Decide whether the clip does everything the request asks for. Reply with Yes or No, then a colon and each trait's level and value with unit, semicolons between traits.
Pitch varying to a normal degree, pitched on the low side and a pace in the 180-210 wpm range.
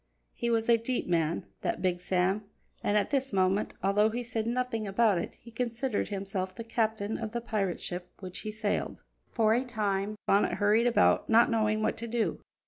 No: average, 3.0 semitones; high, 215 Hz; average, 195 wpm